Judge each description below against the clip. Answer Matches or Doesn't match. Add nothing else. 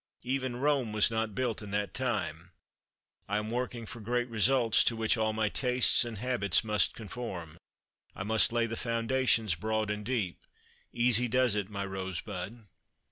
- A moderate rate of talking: Matches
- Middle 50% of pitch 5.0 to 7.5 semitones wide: Doesn't match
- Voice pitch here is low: Matches